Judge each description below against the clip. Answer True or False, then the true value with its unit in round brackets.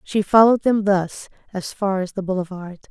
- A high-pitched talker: True (195 Hz)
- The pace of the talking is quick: False (185 wpm)